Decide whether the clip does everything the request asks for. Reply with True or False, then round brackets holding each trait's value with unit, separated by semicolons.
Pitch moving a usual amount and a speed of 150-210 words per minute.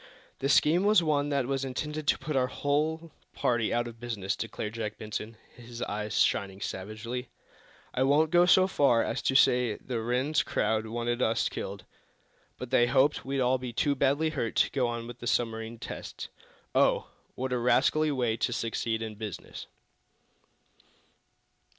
True (3.8 semitones; 170 wpm)